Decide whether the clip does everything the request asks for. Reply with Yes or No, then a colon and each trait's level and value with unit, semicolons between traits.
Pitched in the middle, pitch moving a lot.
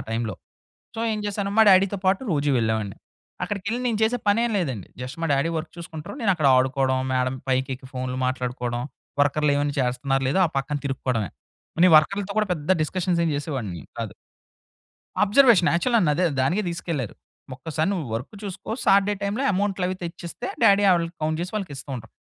Yes: medium, 160 Hz; wide, 6.8 semitones